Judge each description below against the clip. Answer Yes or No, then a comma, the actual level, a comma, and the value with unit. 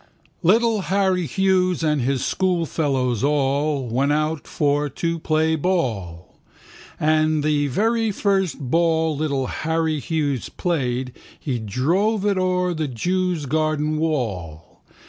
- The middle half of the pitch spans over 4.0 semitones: Yes, average, 4.7 semitones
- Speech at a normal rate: No, slow, 120 wpm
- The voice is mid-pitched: Yes, medium, 155 Hz